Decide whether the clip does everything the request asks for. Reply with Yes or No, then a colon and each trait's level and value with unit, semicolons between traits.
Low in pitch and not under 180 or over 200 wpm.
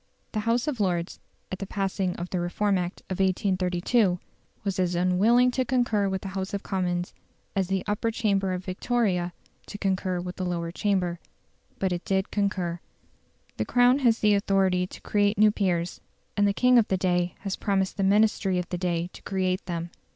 No: high, 190 Hz; average, 190 wpm